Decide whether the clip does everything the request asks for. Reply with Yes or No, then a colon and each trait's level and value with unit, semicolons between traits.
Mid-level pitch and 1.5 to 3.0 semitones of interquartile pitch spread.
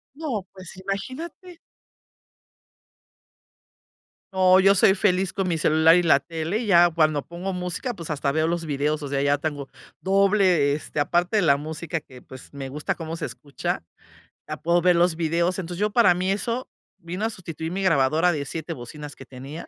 No: medium, 170 Hz; average, 3.8 semitones